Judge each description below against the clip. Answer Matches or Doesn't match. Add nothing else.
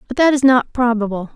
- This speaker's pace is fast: Matches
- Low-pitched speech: Doesn't match